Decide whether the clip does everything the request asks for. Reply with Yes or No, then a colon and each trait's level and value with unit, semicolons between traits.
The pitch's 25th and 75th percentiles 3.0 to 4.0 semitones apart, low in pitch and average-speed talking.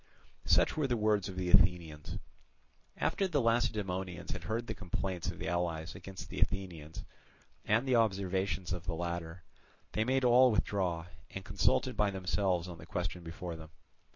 Yes: average, 3.6 semitones; very low, 95 Hz; average, 165 wpm